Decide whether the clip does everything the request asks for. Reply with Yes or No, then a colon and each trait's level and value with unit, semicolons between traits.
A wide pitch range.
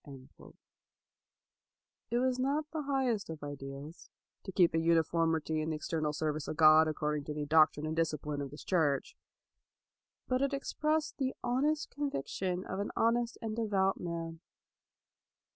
Yes: wide, 7.8 semitones